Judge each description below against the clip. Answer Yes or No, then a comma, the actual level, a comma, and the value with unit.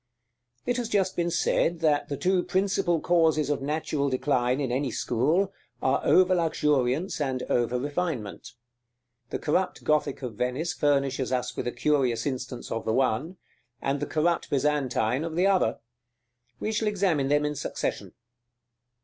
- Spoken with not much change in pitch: No, average, 5.0 semitones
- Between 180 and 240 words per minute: No, average, 160 wpm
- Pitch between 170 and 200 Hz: No, medium, 145 Hz